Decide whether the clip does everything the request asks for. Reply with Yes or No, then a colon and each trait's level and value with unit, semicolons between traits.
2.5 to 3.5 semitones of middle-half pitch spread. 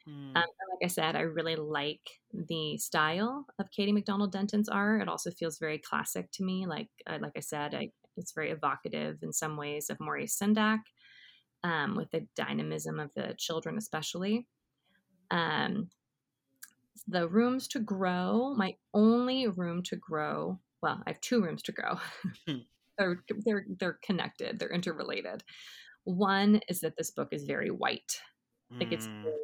No: wide, 5.6 semitones